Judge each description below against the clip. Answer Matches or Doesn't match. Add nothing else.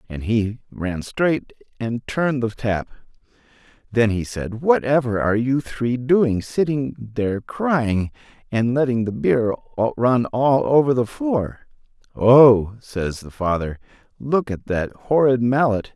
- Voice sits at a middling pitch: Doesn't match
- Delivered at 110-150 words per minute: Matches